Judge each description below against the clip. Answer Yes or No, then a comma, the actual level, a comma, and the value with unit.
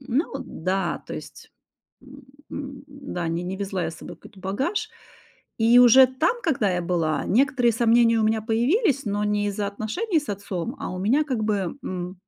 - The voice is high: Yes, high, 220 Hz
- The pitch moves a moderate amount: No, wide, 5.8 semitones